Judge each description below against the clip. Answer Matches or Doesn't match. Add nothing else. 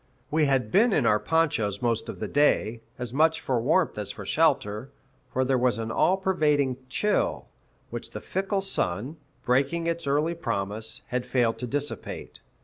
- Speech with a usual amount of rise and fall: Doesn't match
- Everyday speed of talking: Matches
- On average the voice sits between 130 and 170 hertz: Matches